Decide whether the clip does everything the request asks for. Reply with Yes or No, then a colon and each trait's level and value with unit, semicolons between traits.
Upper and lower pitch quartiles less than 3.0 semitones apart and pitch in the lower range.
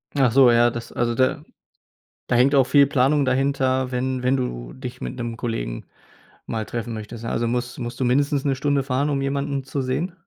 Yes: narrow, 2.5 semitones; low, 130 Hz